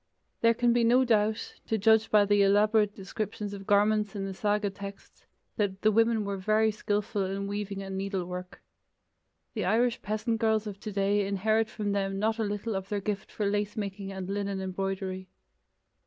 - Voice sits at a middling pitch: No, high, 205 Hz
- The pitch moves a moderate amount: No, narrow, 1.8 semitones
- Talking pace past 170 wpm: Yes, average, 180 wpm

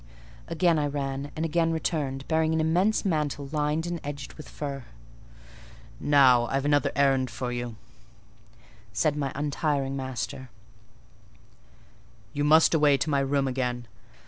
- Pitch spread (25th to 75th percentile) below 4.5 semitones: Yes, narrow, 2.6 semitones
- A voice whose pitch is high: No, medium, 145 Hz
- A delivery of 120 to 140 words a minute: Yes, slow, 135 wpm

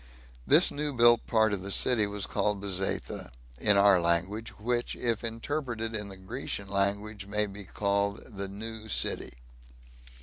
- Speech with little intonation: Yes, narrow, 2.3 semitones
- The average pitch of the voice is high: No, low, 105 Hz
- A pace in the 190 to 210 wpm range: No, average, 155 wpm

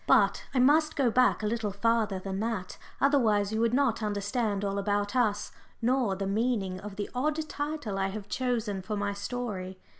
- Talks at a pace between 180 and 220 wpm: Yes, average, 185 wpm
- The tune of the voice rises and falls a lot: No, average, 3.6 semitones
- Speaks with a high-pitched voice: Yes, high, 215 Hz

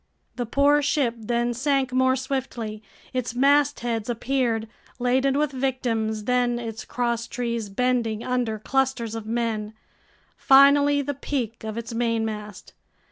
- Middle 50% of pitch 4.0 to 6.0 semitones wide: No, average, 2.9 semitones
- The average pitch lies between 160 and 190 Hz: No, high, 240 Hz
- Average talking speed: No, slow, 125 wpm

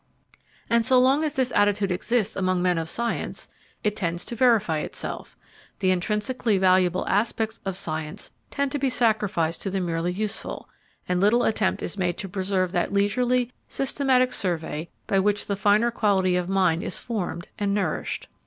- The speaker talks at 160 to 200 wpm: Yes, average, 170 wpm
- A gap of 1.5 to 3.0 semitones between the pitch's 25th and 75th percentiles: No, average, 4.3 semitones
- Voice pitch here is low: No, high, 200 Hz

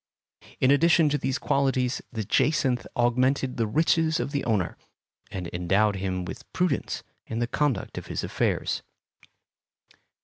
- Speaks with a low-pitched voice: Yes, low, 130 Hz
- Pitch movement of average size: Yes, average, 4.8 semitones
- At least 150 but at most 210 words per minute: No, average, 140 wpm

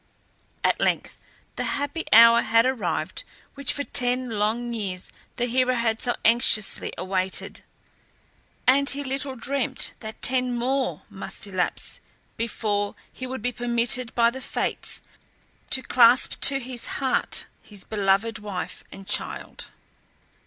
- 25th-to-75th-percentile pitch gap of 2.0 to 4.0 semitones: Yes, average, 2.9 semitones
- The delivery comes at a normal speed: No, slow, 130 wpm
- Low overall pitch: No, high, 240 Hz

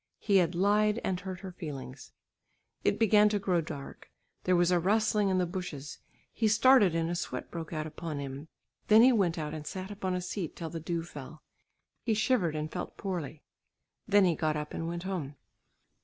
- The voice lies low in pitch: No, medium, 175 Hz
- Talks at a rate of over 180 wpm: Yes, average, 200 wpm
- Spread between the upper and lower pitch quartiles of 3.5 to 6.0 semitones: Yes, average, 4.1 semitones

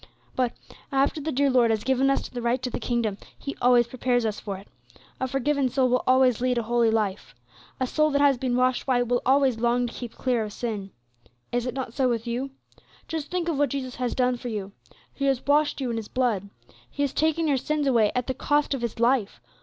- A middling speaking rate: No, fast, 235 wpm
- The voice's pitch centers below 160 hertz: No, very high, 250 Hz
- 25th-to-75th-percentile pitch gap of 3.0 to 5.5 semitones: No, narrow, 2.5 semitones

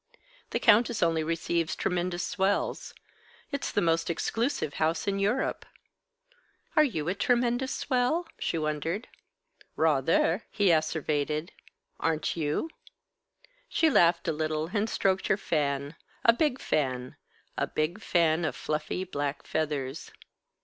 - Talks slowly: Yes, slow, 125 wpm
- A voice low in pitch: No, medium, 170 Hz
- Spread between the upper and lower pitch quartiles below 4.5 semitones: No, average, 5.1 semitones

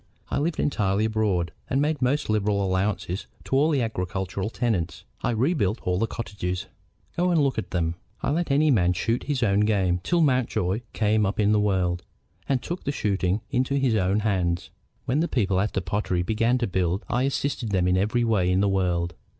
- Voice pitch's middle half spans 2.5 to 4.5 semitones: No, wide, 5.4 semitones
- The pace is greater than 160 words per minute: Yes, average, 200 wpm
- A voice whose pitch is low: Yes, low, 105 Hz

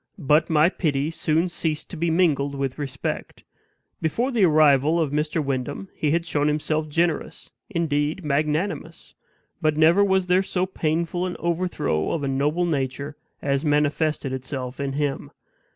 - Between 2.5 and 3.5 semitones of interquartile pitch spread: Yes, average, 3.0 semitones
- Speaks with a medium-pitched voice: Yes, medium, 155 Hz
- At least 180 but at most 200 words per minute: No, average, 150 wpm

